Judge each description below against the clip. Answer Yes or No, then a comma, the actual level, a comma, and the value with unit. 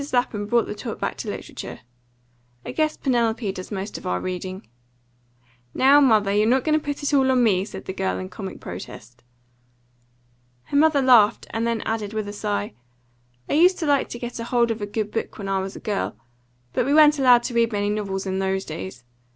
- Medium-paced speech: No, fast, 210 wpm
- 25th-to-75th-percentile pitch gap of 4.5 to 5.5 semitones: Yes, average, 4.9 semitones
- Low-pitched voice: No, high, 220 Hz